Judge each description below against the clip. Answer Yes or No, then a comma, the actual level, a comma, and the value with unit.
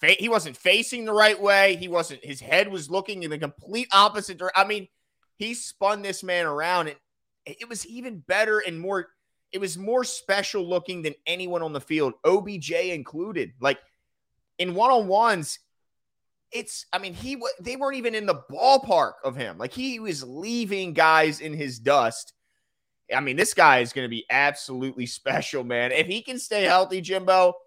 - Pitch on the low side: No, high, 190 Hz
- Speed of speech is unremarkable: Yes, average, 185 wpm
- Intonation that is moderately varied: Yes, average, 5.0 semitones